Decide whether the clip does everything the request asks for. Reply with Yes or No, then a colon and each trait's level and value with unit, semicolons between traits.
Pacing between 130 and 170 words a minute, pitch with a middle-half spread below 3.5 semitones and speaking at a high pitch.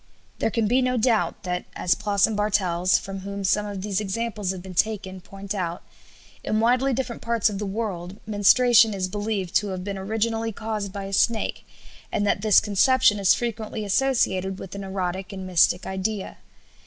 No: average, 185 wpm; average, 2.7 semitones; high, 205 Hz